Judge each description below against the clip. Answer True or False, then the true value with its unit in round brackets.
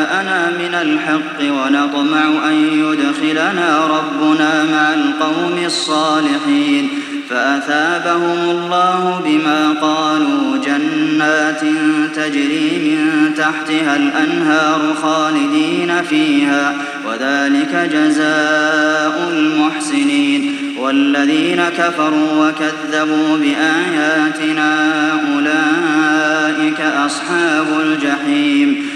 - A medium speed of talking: False (60 wpm)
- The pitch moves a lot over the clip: False (2.6 semitones)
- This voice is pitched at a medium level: True (155 Hz)